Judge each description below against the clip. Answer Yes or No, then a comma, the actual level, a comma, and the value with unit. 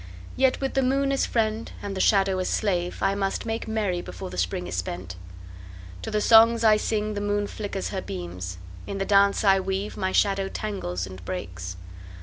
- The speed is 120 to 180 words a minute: No, average, 195 wpm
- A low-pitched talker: No, high, 195 Hz